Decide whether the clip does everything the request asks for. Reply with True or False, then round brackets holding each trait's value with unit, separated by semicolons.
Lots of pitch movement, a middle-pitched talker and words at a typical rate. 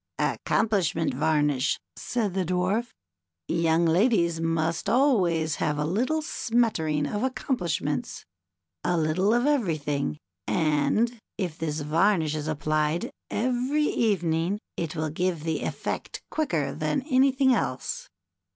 False (6.6 semitones; 170 Hz; 120 wpm)